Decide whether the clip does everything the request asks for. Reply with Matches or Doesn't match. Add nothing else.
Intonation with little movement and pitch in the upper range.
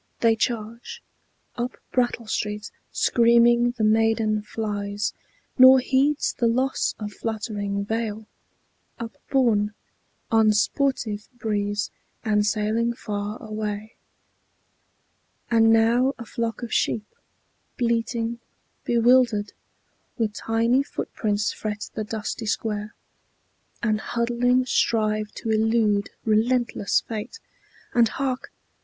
Matches